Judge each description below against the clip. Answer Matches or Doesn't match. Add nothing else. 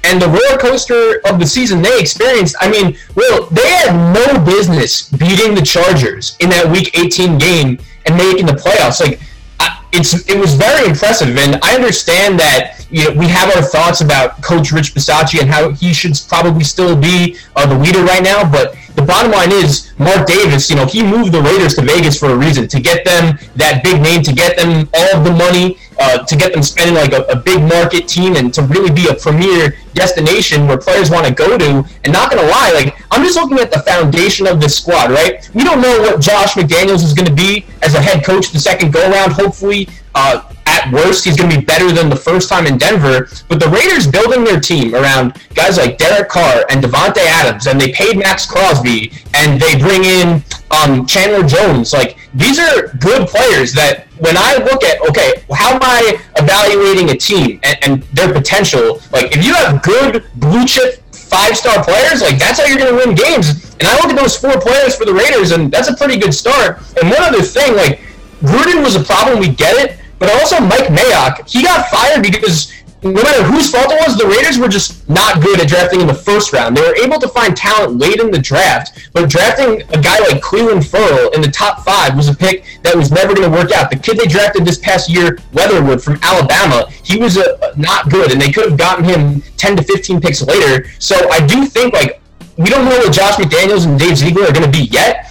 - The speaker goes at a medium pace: Doesn't match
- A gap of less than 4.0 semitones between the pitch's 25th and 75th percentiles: Doesn't match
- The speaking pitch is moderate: Matches